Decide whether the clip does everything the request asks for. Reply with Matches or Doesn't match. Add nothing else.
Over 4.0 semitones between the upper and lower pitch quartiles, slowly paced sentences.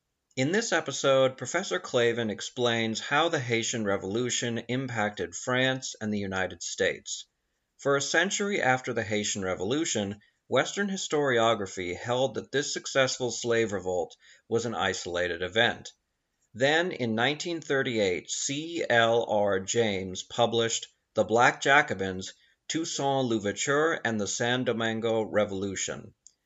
Matches